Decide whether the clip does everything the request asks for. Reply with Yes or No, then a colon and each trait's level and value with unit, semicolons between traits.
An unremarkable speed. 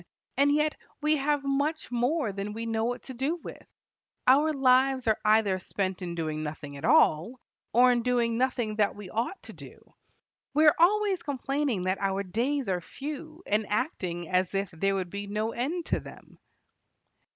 Yes: average, 180 wpm